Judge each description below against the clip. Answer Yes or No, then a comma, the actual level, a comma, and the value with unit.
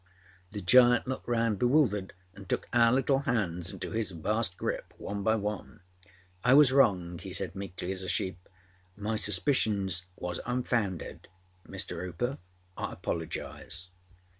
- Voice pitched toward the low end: Yes, low, 105 Hz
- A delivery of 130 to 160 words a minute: Yes, average, 145 wpm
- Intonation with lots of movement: No, average, 4.8 semitones